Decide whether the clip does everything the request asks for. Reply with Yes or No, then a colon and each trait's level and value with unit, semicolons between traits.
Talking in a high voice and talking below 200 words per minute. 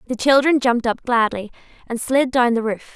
No: high, 245 Hz; fast, 205 wpm